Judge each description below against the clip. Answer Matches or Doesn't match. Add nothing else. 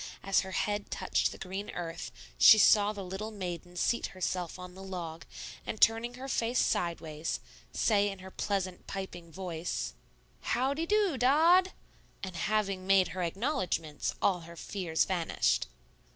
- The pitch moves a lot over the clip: Doesn't match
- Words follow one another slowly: Doesn't match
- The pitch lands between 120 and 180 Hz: Doesn't match